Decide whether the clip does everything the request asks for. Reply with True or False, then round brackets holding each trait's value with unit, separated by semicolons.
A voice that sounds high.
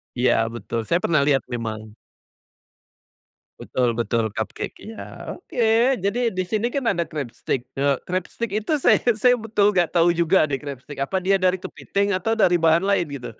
False (175 Hz)